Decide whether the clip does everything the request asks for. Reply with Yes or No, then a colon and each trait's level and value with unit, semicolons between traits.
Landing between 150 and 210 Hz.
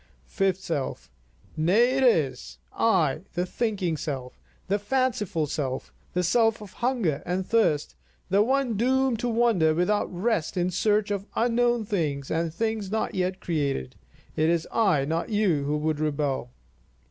Yes: medium, 185 Hz